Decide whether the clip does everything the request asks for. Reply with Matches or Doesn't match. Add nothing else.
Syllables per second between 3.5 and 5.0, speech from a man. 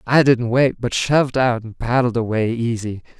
Matches